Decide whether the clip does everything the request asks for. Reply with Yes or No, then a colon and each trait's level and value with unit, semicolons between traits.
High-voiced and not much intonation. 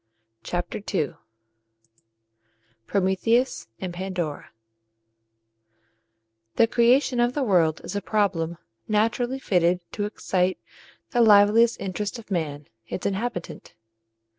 No: high, 200 Hz; average, 4.5 semitones